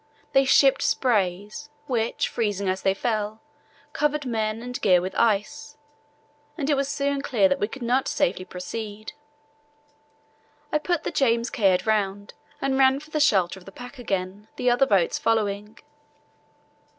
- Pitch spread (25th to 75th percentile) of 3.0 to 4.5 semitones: No, average, 5.2 semitones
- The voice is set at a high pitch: Yes, high, 225 Hz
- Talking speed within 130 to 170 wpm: Yes, average, 155 wpm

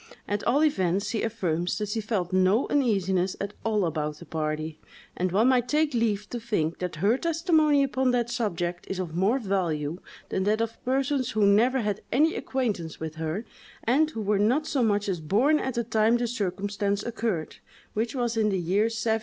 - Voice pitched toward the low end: No, high, 210 Hz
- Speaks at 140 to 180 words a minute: No, average, 195 wpm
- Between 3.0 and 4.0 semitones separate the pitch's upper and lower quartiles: No, average, 4.6 semitones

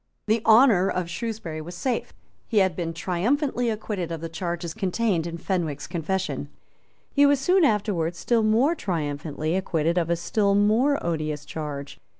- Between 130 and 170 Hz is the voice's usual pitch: No, medium, 180 Hz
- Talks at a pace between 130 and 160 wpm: Yes, average, 155 wpm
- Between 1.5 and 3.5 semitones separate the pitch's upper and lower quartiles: No, average, 5.2 semitones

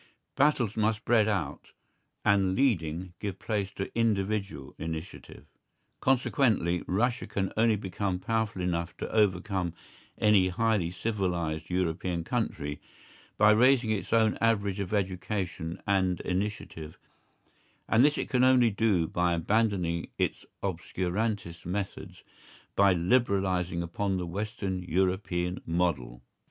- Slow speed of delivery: Yes, slow, 120 wpm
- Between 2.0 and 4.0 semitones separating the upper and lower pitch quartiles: Yes, average, 3.7 semitones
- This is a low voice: Yes, very low, 95 Hz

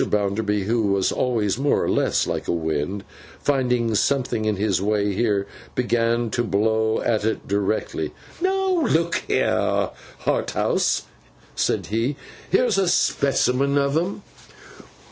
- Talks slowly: Yes, slow, 130 wpm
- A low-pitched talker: Yes, low, 115 Hz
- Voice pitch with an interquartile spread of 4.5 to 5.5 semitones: Yes, average, 5.2 semitones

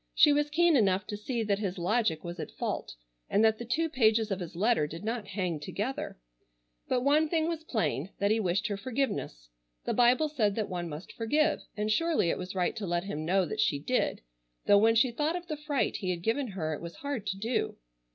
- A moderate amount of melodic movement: No, wide, 6.2 semitones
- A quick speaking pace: Yes, fast, 230 wpm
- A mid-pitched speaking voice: No, high, 215 Hz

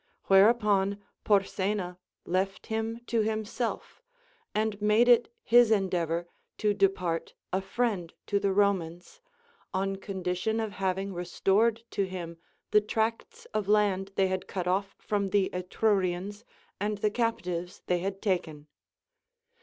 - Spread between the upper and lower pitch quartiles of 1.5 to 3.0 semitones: Yes, narrow, 2.6 semitones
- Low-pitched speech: No, high, 195 Hz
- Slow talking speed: Yes, slow, 130 wpm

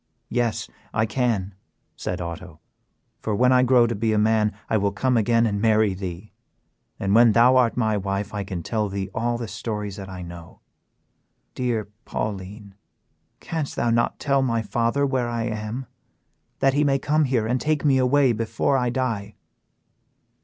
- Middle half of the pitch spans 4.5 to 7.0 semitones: No, average, 3.6 semitones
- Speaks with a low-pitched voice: Yes, low, 115 Hz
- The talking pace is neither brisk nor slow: Yes, average, 175 wpm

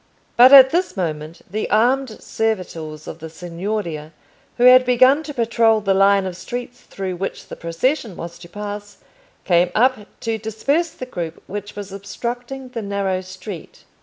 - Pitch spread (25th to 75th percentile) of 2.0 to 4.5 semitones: No, wide, 5.4 semitones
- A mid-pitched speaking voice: No, high, 205 Hz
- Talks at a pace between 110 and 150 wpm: No, average, 165 wpm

